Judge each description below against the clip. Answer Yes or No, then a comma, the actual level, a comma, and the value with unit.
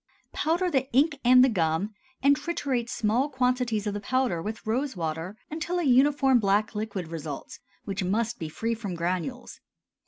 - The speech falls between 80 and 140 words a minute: No, average, 165 wpm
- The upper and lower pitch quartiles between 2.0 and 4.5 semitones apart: No, average, 5.3 semitones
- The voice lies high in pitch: Yes, high, 230 Hz